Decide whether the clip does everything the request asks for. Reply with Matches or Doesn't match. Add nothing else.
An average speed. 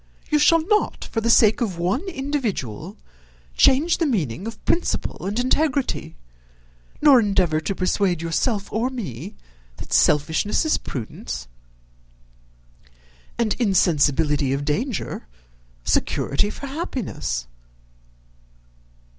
Doesn't match